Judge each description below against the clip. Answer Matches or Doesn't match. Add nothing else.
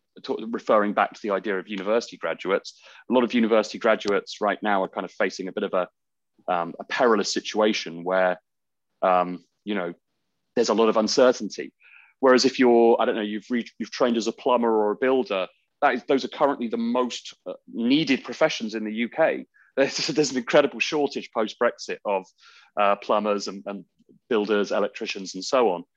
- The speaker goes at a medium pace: Matches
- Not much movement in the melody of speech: Doesn't match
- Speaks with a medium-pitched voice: Doesn't match